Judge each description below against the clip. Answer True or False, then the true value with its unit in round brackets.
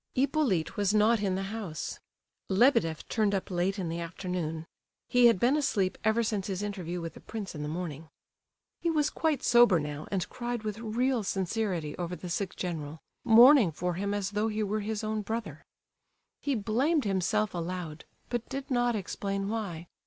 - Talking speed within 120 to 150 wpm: False (175 wpm)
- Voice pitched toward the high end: True (205 Hz)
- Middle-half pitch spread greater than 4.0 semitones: True (4.5 semitones)